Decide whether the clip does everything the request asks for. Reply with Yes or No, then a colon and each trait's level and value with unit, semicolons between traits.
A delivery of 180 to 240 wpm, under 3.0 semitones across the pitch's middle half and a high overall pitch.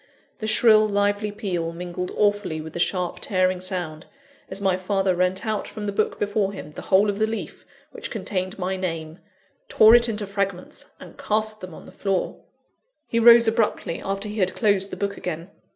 Yes: average, 190 wpm; narrow, 2.6 semitones; high, 195 Hz